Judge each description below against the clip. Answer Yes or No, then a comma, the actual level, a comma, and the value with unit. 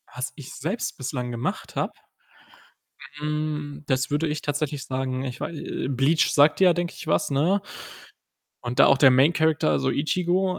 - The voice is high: No, medium, 145 Hz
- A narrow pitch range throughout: No, average, 3.2 semitones